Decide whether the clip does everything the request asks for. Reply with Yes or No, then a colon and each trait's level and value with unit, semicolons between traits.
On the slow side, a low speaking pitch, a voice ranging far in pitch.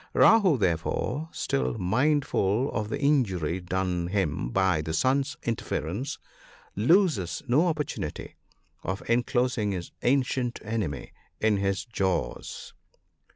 Yes: slow, 110 wpm; low, 105 Hz; wide, 6.3 semitones